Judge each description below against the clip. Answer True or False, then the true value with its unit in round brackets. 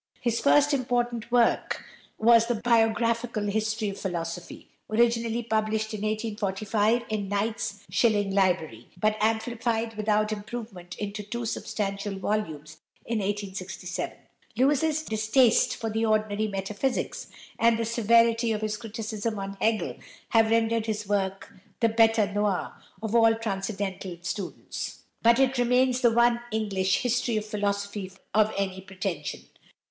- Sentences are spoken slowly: True (130 wpm)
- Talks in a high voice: True (215 Hz)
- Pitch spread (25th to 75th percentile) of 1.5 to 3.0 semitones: True (2.4 semitones)